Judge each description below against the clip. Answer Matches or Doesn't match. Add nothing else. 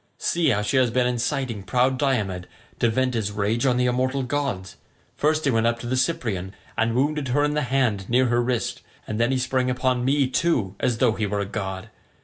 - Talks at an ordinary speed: Doesn't match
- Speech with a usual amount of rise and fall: Matches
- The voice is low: Matches